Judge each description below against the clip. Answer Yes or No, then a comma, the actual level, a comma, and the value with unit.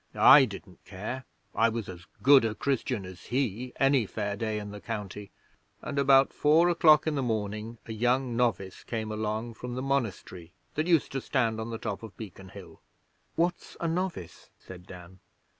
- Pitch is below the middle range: Yes, low, 115 Hz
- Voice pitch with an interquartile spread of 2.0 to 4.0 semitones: No, average, 4.8 semitones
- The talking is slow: No, average, 180 wpm